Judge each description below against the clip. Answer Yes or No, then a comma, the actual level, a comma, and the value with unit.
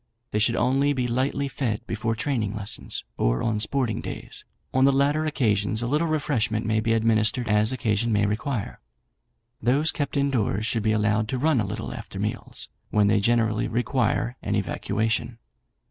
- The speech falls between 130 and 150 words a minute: No, average, 175 wpm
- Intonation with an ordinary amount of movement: Yes, average, 3.6 semitones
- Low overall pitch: Yes, low, 115 Hz